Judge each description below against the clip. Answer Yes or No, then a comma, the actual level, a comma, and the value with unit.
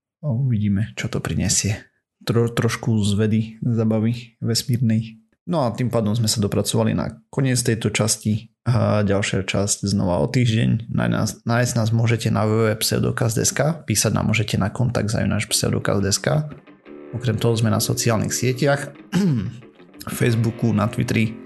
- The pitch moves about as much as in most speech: No, narrow, 2.3 semitones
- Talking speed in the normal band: Yes, average, 135 wpm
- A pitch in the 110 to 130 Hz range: Yes, low, 115 Hz